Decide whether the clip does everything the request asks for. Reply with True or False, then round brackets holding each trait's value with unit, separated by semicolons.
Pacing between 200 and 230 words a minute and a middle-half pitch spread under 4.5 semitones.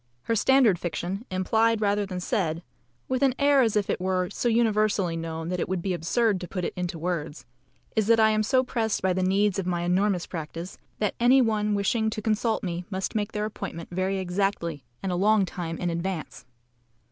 True (205 wpm; 3.5 semitones)